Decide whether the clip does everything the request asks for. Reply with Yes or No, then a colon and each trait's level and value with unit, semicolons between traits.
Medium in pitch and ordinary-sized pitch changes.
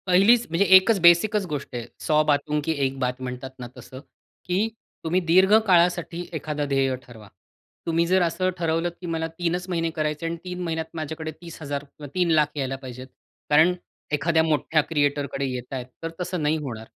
Yes: medium, 160 Hz; average, 3.6 semitones